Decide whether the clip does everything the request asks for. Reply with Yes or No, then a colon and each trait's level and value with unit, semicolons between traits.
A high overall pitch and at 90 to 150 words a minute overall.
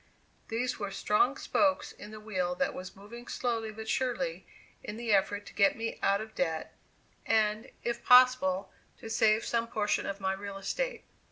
No: high, 220 Hz; average, 175 wpm